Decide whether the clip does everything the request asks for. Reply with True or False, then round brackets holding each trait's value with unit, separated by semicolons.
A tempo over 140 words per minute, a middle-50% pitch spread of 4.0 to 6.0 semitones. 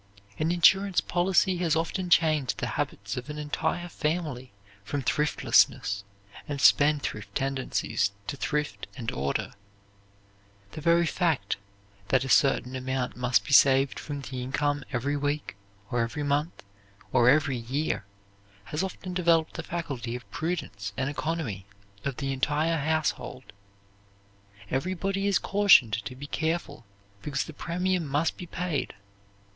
False (135 wpm; 4.3 semitones)